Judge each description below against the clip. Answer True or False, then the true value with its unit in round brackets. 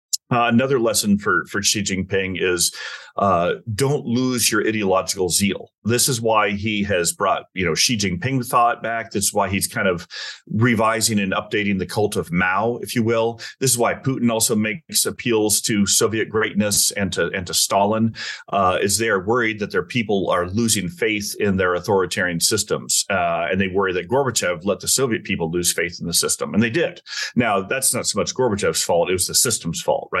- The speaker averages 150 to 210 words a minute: True (205 wpm)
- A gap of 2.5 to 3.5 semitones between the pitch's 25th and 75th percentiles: True (3.0 semitones)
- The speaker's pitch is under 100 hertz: False (110 Hz)